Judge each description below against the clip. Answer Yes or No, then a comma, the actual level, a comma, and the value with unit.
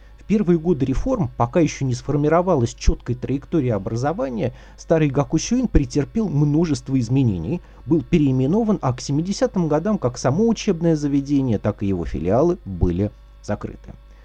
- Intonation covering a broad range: Yes, wide, 5.7 semitones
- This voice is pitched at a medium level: Yes, medium, 145 Hz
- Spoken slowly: No, average, 130 wpm